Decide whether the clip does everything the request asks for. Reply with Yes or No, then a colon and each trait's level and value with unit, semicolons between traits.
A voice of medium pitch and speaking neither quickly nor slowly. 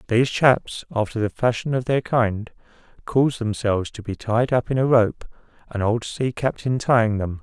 No: low, 115 Hz; average, 185 wpm